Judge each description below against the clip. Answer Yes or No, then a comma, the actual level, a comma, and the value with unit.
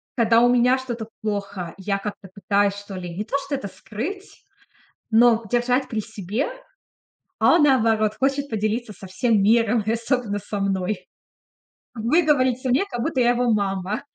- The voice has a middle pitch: No, high, 225 Hz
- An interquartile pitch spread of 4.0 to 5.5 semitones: No, average, 3.6 semitones